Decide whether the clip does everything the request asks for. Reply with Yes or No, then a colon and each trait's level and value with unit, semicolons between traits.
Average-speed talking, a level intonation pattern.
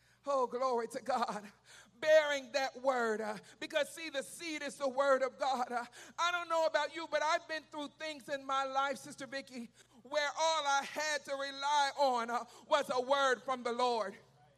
No: average, 195 wpm; average, 3.2 semitones